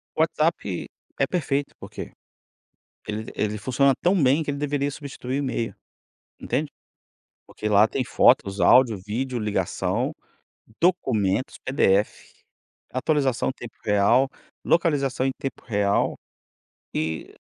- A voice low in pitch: Yes, low, 130 Hz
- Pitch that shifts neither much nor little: Yes, average, 4.9 semitones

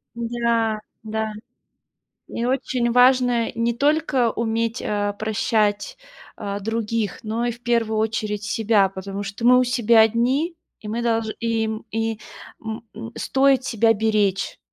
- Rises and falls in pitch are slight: Yes, narrow, 1.7 semitones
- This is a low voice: No, high, 225 Hz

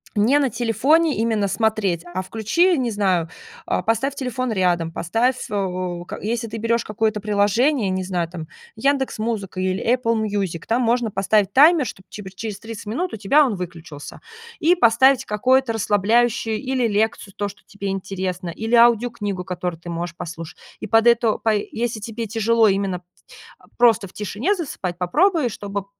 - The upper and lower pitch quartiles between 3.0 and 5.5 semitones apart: Yes, average, 4.0 semitones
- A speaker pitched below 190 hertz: No, high, 215 Hz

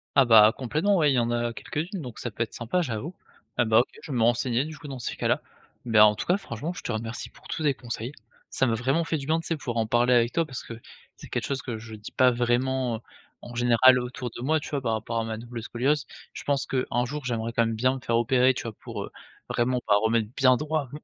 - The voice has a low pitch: Yes, low, 125 Hz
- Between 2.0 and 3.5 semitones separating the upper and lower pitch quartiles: Yes, average, 2.9 semitones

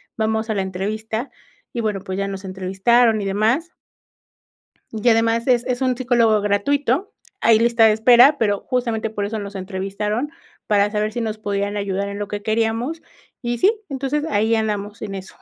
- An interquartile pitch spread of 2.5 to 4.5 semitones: Yes, average, 2.8 semitones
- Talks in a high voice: Yes, high, 220 Hz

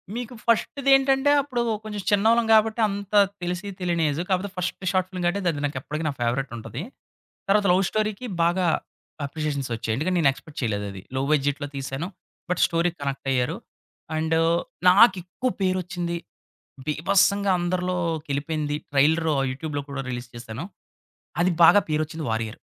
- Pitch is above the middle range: No, medium, 170 Hz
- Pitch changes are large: Yes, wide, 5.7 semitones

